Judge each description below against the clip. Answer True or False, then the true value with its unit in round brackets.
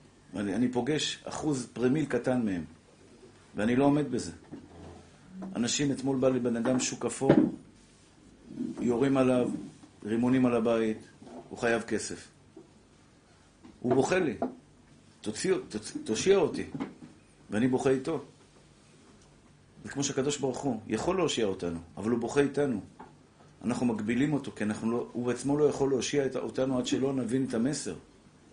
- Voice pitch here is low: True (130 Hz)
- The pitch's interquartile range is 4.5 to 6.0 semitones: False (3.3 semitones)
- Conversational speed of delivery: True (135 wpm)